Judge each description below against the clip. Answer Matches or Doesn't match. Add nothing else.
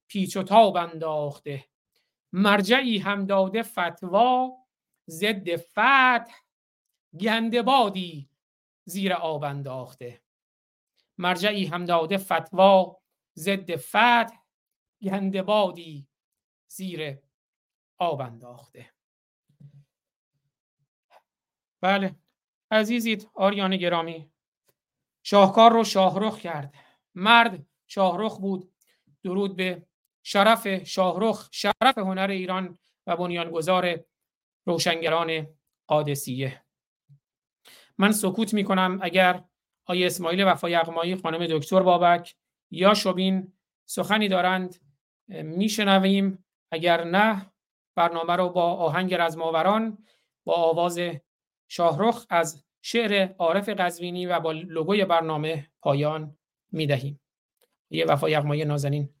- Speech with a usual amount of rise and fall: Matches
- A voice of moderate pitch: Matches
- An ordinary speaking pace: Doesn't match